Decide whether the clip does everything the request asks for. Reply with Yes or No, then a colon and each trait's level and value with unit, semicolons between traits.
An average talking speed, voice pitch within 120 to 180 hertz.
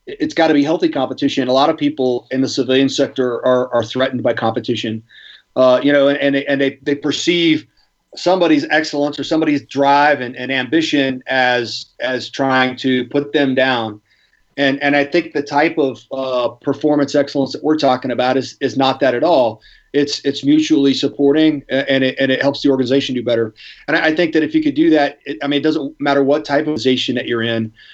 No: fast, 215 wpm; medium, 140 Hz